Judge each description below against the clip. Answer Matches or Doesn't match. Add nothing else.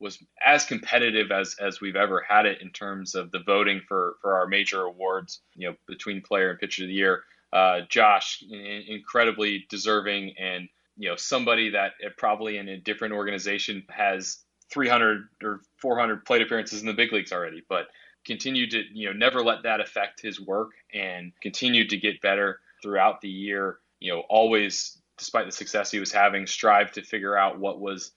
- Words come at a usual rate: Matches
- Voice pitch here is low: Matches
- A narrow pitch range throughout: Matches